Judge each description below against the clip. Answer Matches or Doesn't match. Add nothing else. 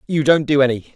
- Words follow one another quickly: Matches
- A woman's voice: Doesn't match